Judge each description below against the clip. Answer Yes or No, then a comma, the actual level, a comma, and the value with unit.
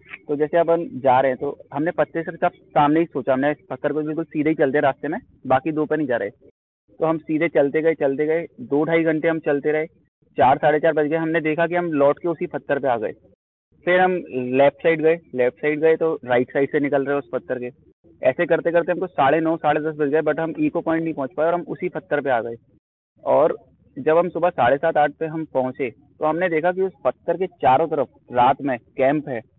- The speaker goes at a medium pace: No, fast, 245 wpm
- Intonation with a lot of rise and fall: No, average, 2.7 semitones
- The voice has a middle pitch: Yes, medium, 155 Hz